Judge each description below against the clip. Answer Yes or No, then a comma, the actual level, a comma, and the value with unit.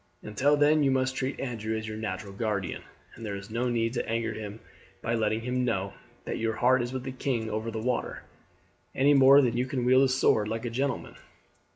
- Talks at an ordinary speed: No, fast, 225 wpm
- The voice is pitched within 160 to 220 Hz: No, low, 115 Hz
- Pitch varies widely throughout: No, average, 3.1 semitones